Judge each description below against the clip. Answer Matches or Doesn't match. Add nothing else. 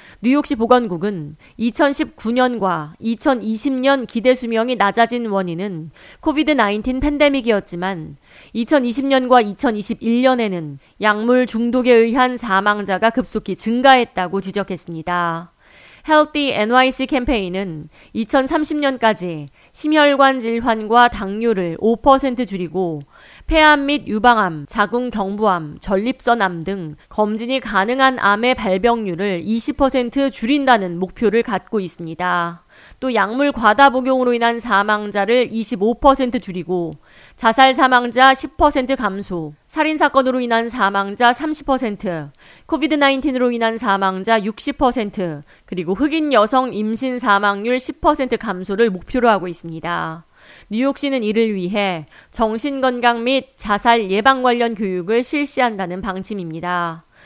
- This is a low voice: Doesn't match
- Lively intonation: Doesn't match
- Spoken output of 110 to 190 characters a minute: Doesn't match